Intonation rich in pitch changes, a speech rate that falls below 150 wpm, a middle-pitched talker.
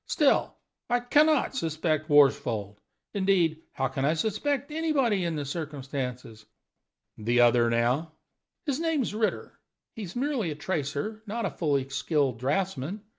Yes: wide, 8.6 semitones; average, 140 wpm; medium, 160 Hz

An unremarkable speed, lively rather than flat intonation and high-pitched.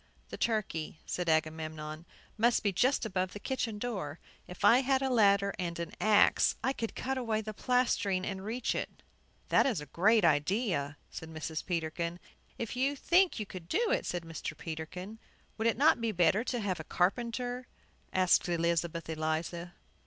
Yes: average, 175 wpm; wide, 5.8 semitones; high, 195 Hz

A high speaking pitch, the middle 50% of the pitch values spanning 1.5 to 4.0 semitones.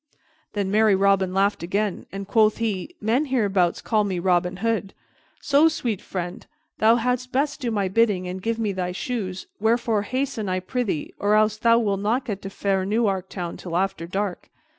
Yes: high, 205 Hz; average, 3.4 semitones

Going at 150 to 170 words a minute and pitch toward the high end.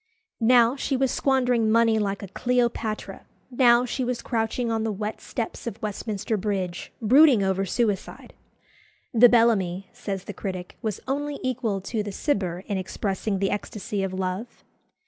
Yes: average, 155 wpm; high, 220 Hz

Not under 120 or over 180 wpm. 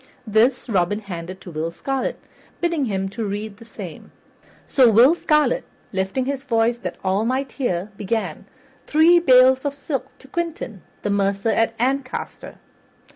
Yes: average, 150 wpm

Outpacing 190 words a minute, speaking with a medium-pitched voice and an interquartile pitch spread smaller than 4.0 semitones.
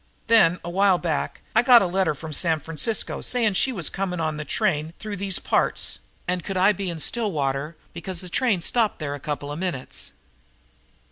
No: average, 200 wpm; medium, 180 Hz; average, 4.3 semitones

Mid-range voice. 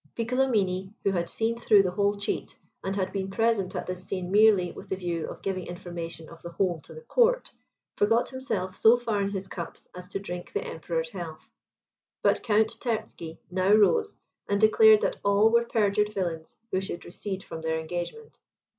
No: high, 200 Hz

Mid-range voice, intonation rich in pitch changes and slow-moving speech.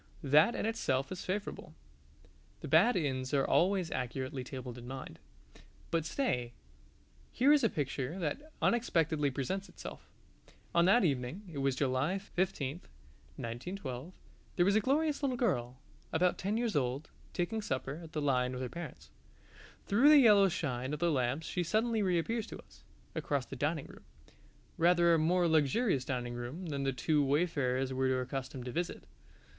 No: medium, 155 Hz; wide, 6.5 semitones; average, 160 wpm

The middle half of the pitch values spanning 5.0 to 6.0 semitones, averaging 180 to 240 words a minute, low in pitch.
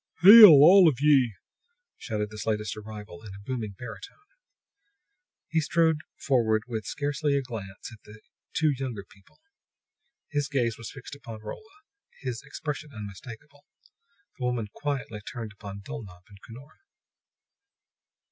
No: average, 5.3 semitones; slow, 135 wpm; low, 120 Hz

